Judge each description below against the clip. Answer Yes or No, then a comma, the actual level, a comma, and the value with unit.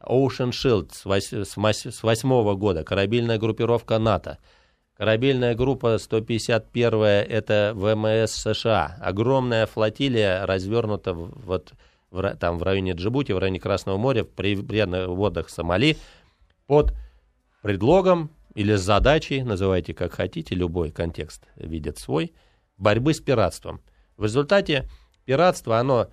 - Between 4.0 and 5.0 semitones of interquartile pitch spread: Yes, average, 4.5 semitones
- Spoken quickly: No, average, 115 wpm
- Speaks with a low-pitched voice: Yes, low, 105 Hz